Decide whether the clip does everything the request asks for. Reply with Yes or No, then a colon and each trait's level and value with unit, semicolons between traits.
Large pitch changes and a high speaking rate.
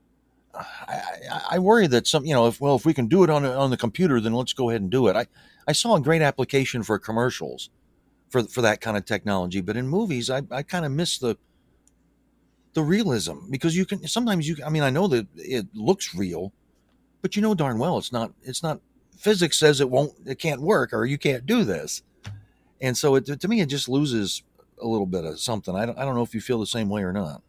Yes: wide, 6.2 semitones; fast, 240 wpm